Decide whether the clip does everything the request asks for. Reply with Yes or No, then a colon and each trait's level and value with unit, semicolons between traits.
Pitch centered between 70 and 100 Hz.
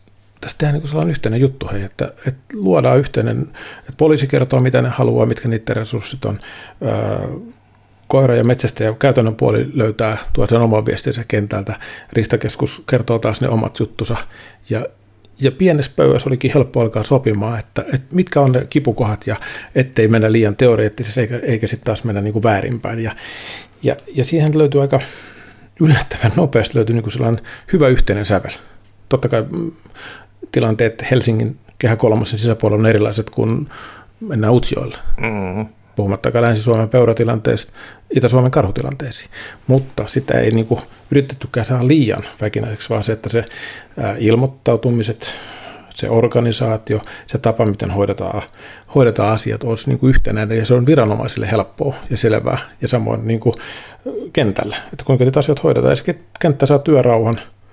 No: low, 115 Hz